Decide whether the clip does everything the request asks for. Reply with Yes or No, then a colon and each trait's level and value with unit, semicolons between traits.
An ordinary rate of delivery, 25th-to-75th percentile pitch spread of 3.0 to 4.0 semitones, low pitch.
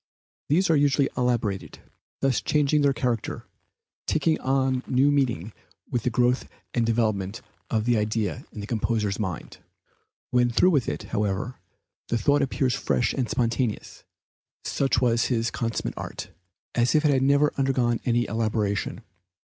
Yes: average, 145 wpm; average, 3.3 semitones; low, 120 Hz